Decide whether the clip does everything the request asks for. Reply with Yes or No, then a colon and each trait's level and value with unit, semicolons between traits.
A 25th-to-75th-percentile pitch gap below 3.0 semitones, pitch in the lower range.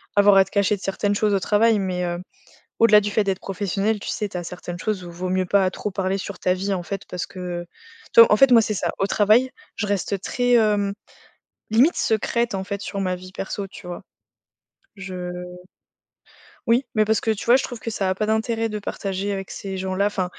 No: narrow, 2.4 semitones; high, 200 Hz